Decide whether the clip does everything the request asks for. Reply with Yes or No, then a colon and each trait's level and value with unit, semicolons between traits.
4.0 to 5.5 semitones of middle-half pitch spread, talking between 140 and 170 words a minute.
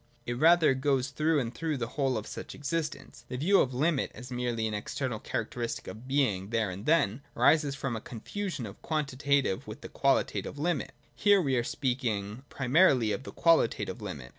No: average, 4.5 semitones; average, 180 wpm